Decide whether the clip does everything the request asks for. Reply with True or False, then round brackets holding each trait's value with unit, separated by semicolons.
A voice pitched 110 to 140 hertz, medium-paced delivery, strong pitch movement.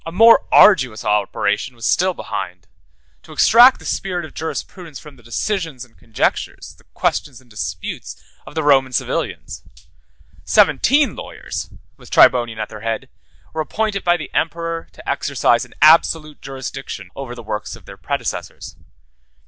True (135 Hz; 150 wpm; 6.7 semitones)